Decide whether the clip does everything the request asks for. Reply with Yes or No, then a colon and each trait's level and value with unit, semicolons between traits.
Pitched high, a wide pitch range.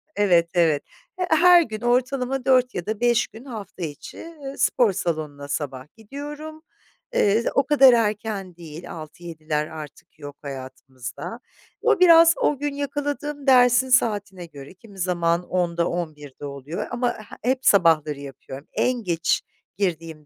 Yes: high, 200 Hz; wide, 8.4 semitones